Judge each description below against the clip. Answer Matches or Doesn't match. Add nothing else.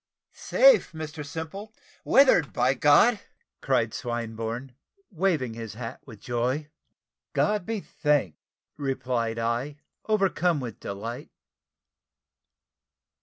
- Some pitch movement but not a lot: Doesn't match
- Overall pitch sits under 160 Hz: Matches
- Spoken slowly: Matches